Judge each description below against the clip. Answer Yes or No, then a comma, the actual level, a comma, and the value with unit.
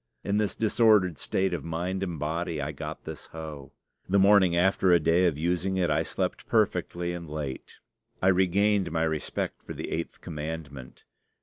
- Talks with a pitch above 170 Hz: No, very low, 85 Hz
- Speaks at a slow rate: No, average, 175 wpm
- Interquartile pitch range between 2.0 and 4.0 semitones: Yes, average, 3.1 semitones